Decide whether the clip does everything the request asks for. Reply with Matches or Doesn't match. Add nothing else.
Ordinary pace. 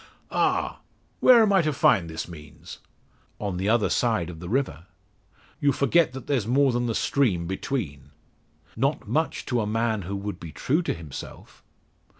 Matches